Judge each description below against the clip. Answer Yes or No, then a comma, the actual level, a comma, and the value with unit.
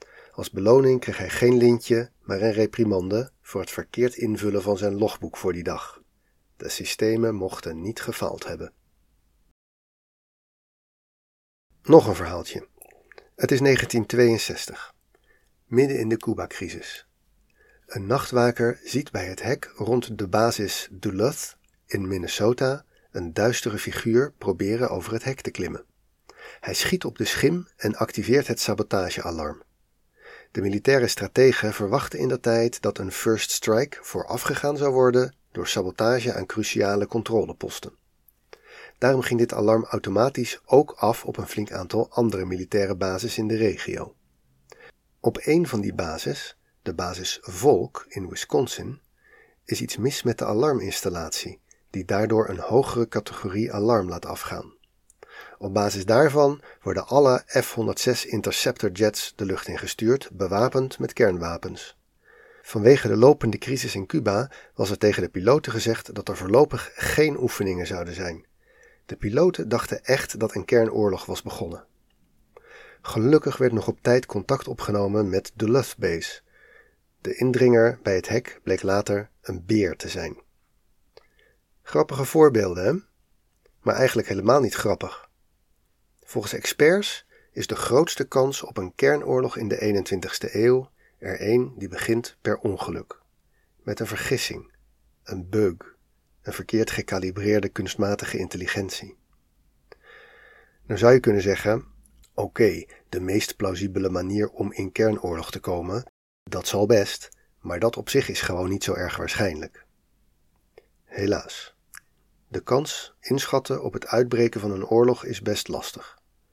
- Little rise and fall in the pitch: No, average, 4.1 semitones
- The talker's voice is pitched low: Yes, low, 110 Hz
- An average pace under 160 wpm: Yes, average, 140 wpm